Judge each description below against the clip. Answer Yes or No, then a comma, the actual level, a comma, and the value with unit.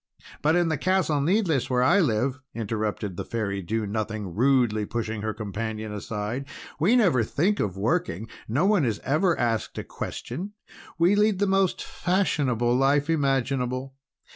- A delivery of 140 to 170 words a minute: Yes, average, 155 wpm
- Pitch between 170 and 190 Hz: No, low, 130 Hz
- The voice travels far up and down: Yes, wide, 7.2 semitones